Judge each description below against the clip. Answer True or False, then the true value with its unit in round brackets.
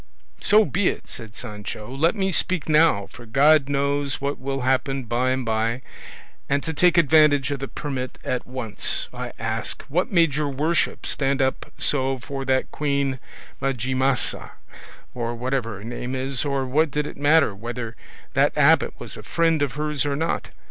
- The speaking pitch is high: False (135 Hz)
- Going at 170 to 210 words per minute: True (175 wpm)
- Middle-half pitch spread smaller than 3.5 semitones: True (2.8 semitones)